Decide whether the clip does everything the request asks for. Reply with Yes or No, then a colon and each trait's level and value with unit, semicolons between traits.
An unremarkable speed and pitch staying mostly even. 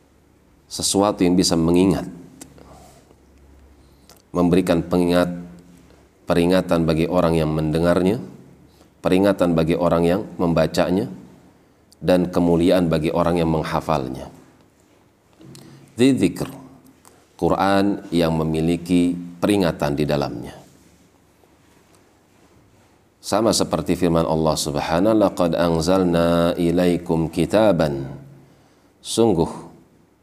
No: slow, 80 wpm; narrow, 1.8 semitones